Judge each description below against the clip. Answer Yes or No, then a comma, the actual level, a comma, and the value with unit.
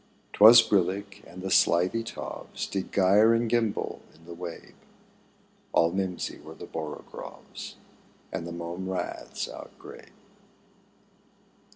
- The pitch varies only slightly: No, average, 3.4 semitones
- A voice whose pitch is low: Yes, very low, 95 Hz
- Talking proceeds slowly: Yes, slow, 115 wpm